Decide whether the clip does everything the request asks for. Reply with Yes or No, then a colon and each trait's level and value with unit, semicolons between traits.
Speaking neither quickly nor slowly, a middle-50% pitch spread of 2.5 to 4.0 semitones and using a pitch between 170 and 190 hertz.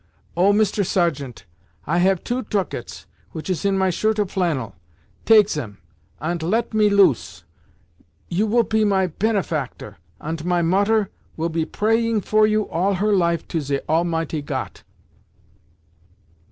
No: average, 145 wpm; average, 4.4 semitones; medium, 185 Hz